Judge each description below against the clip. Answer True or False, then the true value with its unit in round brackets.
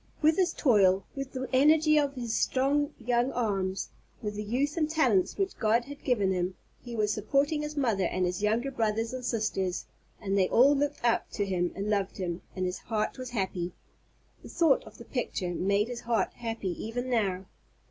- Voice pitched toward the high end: True (230 Hz)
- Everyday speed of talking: True (195 wpm)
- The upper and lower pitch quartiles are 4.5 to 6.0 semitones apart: True (5.6 semitones)